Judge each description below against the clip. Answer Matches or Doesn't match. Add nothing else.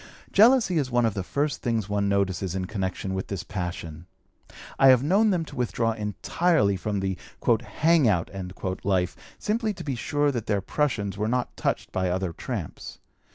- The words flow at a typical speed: Matches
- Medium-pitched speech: Doesn't match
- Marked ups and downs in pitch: Matches